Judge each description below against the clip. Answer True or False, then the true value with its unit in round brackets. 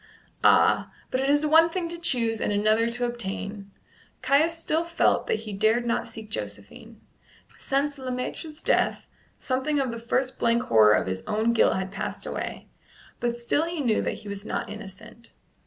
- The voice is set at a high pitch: True (235 Hz)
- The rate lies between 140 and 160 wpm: False (180 wpm)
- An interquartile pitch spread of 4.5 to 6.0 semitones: True (4.8 semitones)